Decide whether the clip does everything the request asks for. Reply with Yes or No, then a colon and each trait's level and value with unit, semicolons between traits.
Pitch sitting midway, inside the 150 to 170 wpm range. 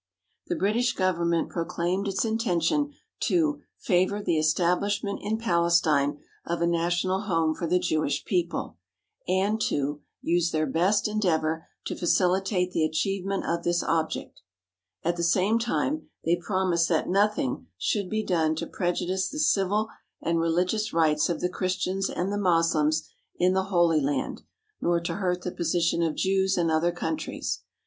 Yes: medium, 175 Hz; average, 155 wpm